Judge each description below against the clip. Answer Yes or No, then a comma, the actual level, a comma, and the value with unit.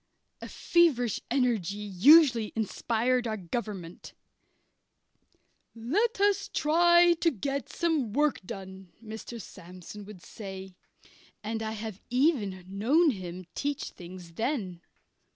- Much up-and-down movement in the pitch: Yes, wide, 6.9 semitones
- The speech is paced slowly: Yes, slow, 110 wpm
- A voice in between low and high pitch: No, high, 225 Hz